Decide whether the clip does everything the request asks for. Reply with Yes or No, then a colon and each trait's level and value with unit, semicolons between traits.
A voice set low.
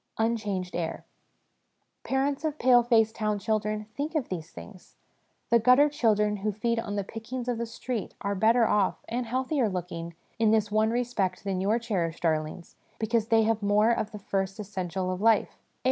No: high, 215 Hz